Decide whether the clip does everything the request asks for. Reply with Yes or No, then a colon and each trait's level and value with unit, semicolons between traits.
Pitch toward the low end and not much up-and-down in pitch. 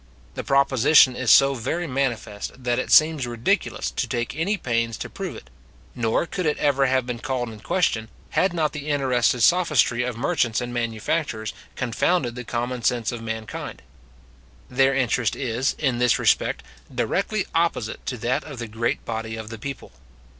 No: low, 125 Hz; average, 3.5 semitones